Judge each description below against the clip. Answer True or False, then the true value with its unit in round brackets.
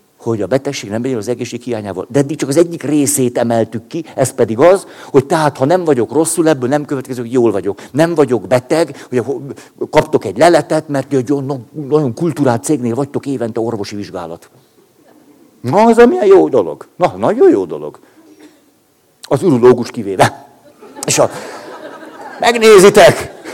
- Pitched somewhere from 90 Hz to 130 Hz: False (140 Hz)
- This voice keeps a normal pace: False (160 wpm)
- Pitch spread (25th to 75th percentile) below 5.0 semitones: False (5.6 semitones)